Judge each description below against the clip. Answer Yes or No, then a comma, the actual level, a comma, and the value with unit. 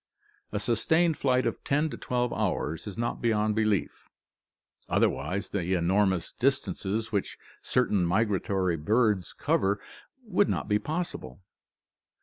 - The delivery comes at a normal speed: No, slow, 125 wpm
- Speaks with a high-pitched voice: No, low, 105 Hz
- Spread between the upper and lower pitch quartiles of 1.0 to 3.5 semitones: No, average, 4.3 semitones